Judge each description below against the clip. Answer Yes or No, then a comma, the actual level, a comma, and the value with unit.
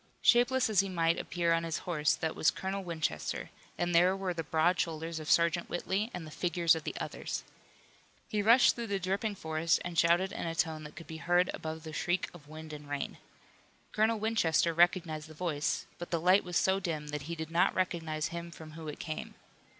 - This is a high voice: No, medium, 170 Hz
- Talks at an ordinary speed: No, fast, 210 wpm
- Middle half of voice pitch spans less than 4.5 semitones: Yes, average, 2.7 semitones